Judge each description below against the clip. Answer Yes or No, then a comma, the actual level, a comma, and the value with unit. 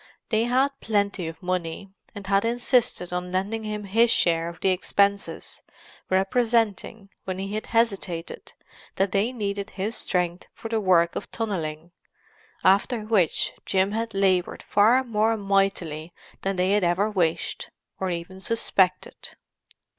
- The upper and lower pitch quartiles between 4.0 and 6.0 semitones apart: No, average, 3.2 semitones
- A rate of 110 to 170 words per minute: Yes, average, 140 wpm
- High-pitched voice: Yes, high, 195 Hz